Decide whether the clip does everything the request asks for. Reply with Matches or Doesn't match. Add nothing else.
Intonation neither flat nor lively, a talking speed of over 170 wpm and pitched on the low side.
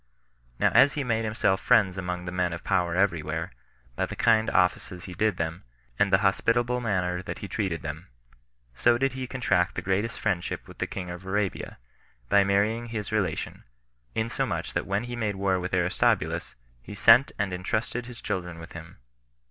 Matches